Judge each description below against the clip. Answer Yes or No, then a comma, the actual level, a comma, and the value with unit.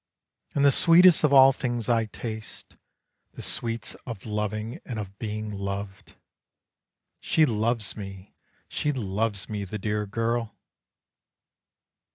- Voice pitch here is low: Yes, low, 110 Hz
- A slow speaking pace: Yes, slow, 125 wpm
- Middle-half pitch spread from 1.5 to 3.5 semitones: Yes, narrow, 2.5 semitones